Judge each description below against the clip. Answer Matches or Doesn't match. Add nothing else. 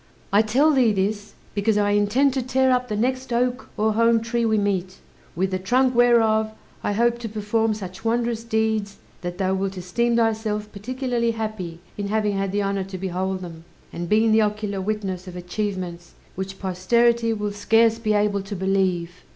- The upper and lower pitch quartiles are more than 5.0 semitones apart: Doesn't match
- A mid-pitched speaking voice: Doesn't match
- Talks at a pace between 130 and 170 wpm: Doesn't match